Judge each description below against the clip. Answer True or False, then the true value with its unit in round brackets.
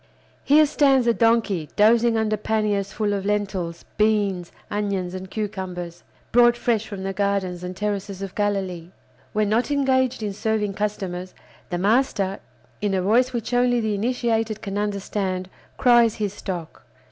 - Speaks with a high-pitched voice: True (205 Hz)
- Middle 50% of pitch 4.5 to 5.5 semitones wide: False (2.9 semitones)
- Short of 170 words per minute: True (150 wpm)